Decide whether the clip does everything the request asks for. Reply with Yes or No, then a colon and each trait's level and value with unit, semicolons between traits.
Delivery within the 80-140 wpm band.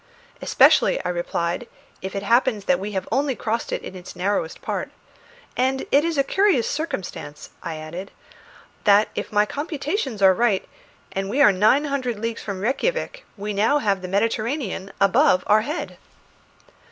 No: average, 165 wpm